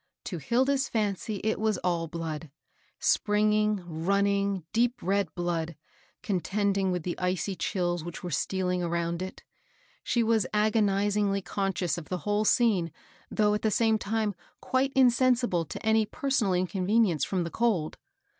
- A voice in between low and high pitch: No, high, 200 Hz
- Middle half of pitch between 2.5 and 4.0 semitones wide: Yes, average, 3.7 semitones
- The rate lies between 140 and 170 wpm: Yes, average, 150 wpm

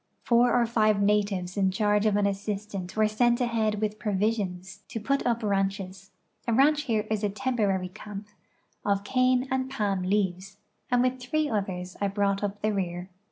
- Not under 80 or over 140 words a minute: No, average, 175 wpm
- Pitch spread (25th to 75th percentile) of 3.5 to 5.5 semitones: No, average, 3.1 semitones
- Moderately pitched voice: No, high, 210 Hz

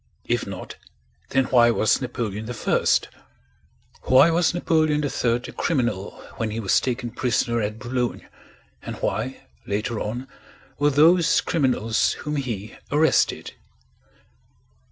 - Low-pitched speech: Yes, low, 125 Hz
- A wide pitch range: No, average, 4.5 semitones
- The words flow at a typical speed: No, slow, 120 wpm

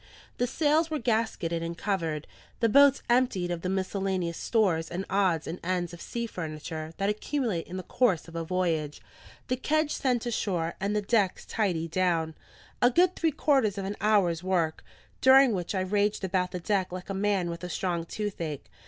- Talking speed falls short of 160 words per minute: No, average, 190 wpm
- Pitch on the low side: No, high, 190 Hz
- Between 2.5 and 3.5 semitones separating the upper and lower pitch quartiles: No, average, 4.9 semitones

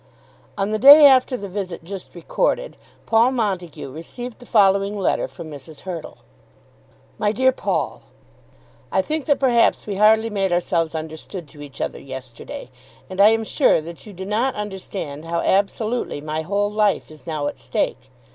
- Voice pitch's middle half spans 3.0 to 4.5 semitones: No, average, 5.3 semitones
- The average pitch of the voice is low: No, high, 195 Hz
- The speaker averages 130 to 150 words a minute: No, average, 165 wpm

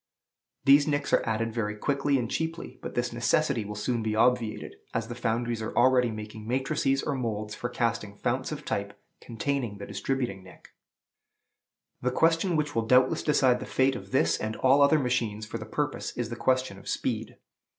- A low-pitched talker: Yes, low, 120 Hz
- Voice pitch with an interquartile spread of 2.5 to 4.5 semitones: Yes, average, 3.7 semitones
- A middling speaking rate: Yes, average, 185 wpm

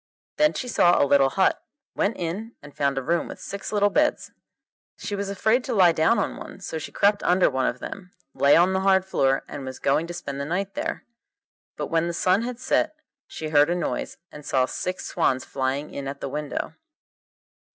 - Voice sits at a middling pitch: Yes, medium, 170 Hz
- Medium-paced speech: No, fast, 215 wpm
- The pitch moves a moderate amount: No, wide, 5.9 semitones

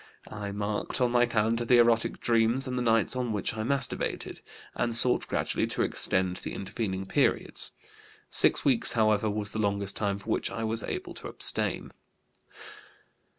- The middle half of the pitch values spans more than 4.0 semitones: No, narrow, 2.5 semitones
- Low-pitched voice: Yes, low, 110 Hz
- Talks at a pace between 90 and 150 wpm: No, average, 165 wpm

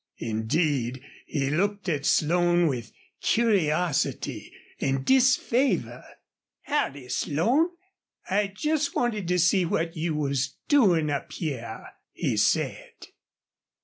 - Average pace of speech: No, slow, 105 wpm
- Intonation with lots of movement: Yes, wide, 6.6 semitones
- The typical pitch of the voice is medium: Yes, medium, 165 Hz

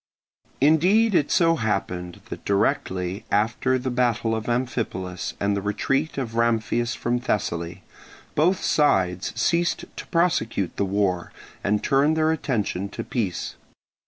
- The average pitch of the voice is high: No, low, 115 Hz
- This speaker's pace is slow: Yes, slow, 130 wpm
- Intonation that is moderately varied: No, wide, 6.4 semitones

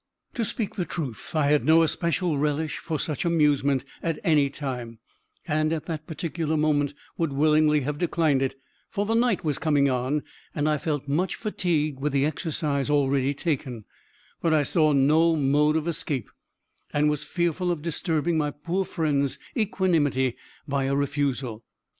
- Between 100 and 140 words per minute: No, average, 165 wpm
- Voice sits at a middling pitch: Yes, medium, 150 Hz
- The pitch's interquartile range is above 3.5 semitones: No, average, 2.7 semitones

